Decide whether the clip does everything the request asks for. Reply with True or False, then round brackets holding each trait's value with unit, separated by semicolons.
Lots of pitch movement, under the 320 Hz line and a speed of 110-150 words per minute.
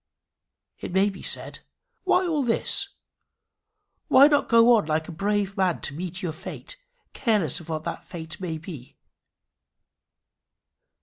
True (6.3 semitones; 190 Hz; 140 wpm)